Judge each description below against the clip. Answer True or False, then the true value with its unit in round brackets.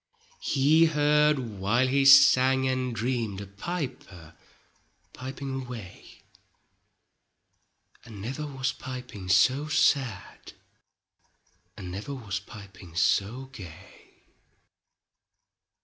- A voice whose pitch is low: True (125 Hz)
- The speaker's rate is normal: False (85 wpm)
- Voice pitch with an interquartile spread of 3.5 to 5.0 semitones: False (5.4 semitones)